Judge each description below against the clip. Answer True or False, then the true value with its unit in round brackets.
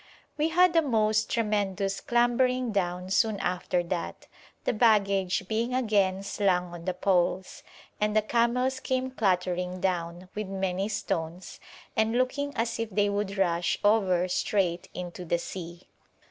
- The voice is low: False (200 Hz)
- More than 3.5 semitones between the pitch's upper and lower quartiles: True (4.0 semitones)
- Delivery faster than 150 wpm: False (145 wpm)